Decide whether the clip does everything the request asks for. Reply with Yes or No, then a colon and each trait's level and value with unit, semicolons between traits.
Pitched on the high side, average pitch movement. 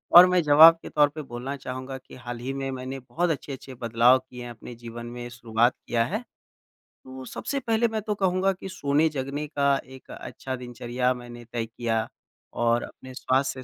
No: low, 130 Hz; average, 3.5 semitones